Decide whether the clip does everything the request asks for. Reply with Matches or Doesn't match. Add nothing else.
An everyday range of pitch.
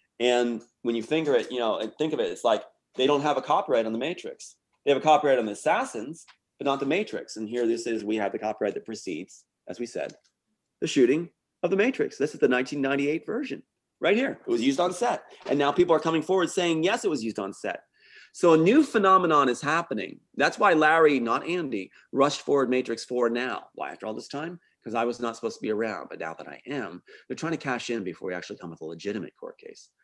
Doesn't match